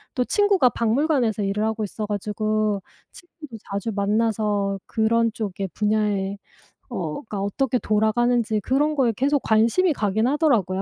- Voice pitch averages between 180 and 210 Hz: No, high, 220 Hz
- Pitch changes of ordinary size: Yes, average, 3.3 semitones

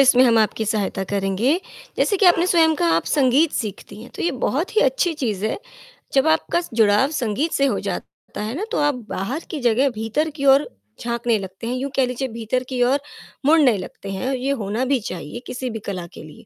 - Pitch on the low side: No, very high, 250 Hz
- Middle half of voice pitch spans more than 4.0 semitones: Yes, average, 5.0 semitones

